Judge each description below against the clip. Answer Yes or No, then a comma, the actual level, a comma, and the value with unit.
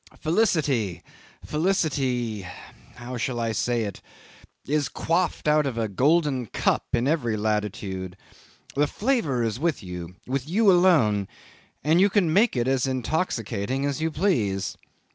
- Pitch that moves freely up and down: Yes, wide, 6.4 semitones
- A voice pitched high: No, low, 130 Hz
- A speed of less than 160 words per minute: Yes, average, 140 wpm